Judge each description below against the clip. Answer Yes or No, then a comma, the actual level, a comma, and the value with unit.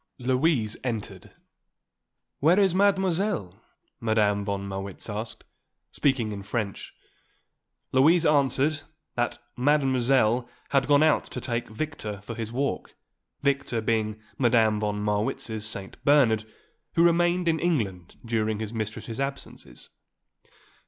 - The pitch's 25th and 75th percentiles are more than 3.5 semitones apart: Yes, average, 5.2 semitones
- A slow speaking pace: Yes, slow, 115 wpm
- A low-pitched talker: Yes, low, 120 Hz